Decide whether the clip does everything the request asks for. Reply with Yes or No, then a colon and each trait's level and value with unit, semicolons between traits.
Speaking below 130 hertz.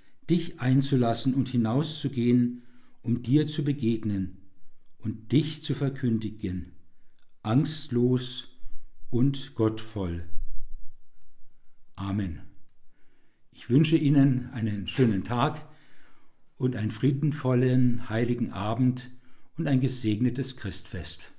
Yes: low, 120 Hz